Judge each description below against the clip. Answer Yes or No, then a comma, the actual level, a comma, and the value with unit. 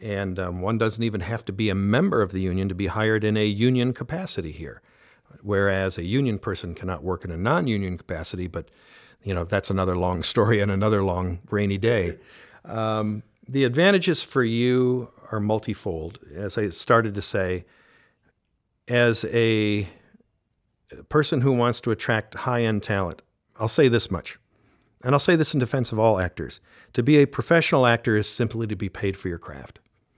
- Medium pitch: No, low, 110 Hz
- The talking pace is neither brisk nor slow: Yes, average, 180 wpm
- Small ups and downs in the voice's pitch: No, average, 3.9 semitones